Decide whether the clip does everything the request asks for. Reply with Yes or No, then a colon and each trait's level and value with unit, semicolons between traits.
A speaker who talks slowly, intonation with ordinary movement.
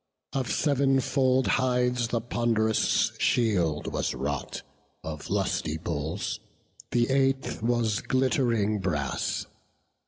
Yes: slow, 100 wpm; average, 4.1 semitones